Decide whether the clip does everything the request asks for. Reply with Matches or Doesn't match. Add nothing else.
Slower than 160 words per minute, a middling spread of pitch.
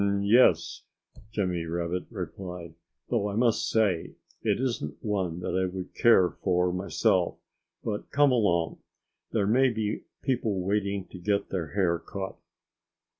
Matches